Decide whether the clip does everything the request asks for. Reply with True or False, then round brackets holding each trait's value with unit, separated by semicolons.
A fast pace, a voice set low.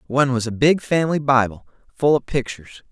False (185 wpm; 130 Hz)